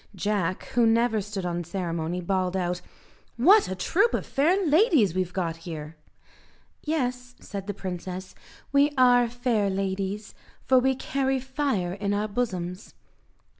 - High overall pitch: Yes, high, 205 Hz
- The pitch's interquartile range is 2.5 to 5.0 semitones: No, wide, 5.6 semitones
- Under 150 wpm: Yes, average, 140 wpm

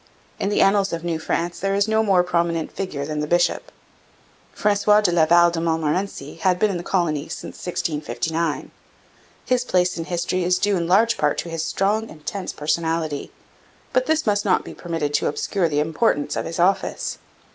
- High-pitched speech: No, medium, 175 Hz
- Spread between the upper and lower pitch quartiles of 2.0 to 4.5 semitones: Yes, average, 3.5 semitones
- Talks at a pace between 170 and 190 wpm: Yes, average, 185 wpm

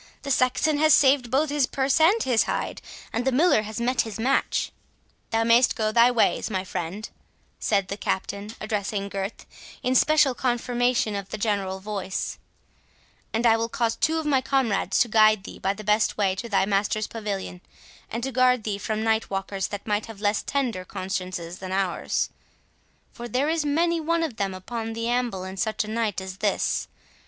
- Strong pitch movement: No, average, 4.2 semitones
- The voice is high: Yes, high, 220 Hz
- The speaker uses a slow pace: No, average, 190 wpm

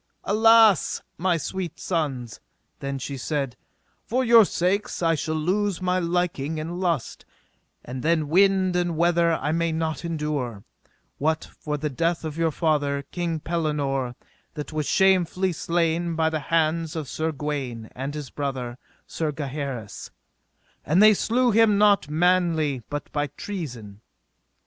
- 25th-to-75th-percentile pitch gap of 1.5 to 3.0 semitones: No, average, 3.6 semitones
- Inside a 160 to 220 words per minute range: No, average, 145 wpm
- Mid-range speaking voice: Yes, medium, 160 Hz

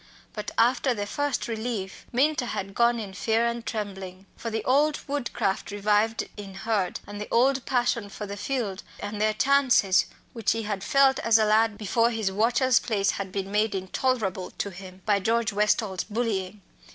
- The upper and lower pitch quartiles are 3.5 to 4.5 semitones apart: No, average, 3.1 semitones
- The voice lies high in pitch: Yes, high, 215 Hz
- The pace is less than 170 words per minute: No, average, 175 wpm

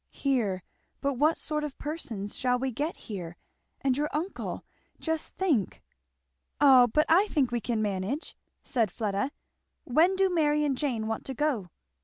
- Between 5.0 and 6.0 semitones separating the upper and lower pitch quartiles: Yes, average, 5.3 semitones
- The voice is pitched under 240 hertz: No, very high, 265 Hz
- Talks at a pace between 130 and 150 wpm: No, average, 160 wpm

